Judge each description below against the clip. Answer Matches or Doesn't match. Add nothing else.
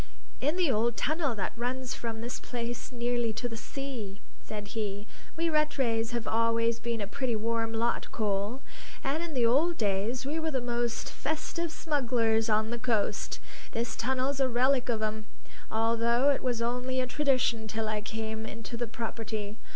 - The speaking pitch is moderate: Doesn't match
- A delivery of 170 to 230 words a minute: Matches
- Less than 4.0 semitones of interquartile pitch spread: Matches